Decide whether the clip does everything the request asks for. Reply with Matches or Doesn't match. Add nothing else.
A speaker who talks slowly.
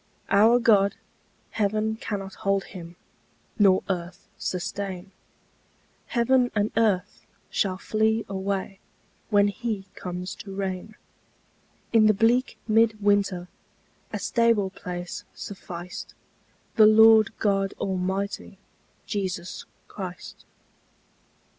Matches